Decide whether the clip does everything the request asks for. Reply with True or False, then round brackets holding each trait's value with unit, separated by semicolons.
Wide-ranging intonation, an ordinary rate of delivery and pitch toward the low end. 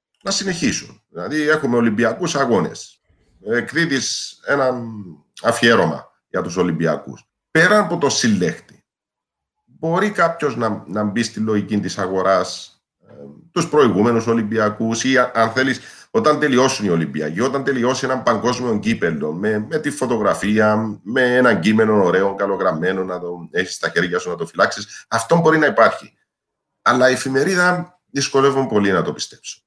True (6.3 semitones; 140 wpm; 125 Hz)